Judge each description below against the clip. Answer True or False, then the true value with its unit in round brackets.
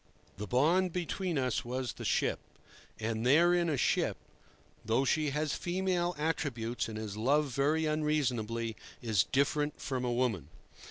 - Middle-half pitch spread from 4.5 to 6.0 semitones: True (5.2 semitones)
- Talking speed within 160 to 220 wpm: False (145 wpm)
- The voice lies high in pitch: False (140 Hz)